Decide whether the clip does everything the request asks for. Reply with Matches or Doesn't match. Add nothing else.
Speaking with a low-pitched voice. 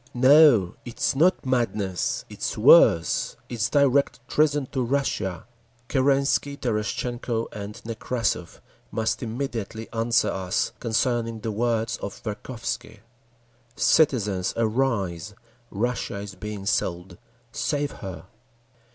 Matches